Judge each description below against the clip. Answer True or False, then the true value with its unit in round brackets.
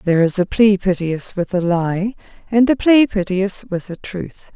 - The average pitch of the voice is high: True (195 Hz)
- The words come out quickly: False (195 wpm)